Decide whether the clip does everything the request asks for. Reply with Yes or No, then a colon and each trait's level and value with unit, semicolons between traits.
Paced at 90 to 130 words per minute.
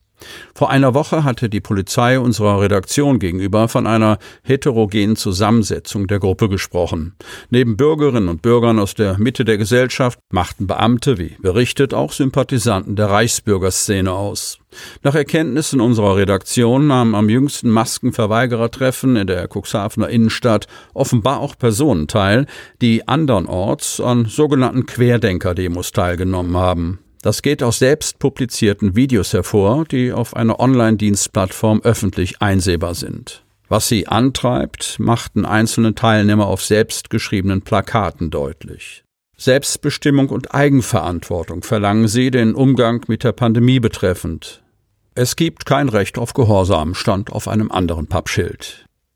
Yes: slow, 125 wpm